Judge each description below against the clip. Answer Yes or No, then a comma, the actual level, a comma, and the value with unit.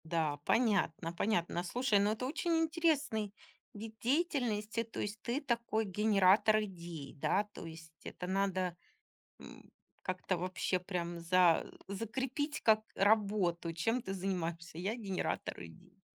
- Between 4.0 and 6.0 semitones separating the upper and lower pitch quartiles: Yes, average, 4.5 semitones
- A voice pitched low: No, high, 200 Hz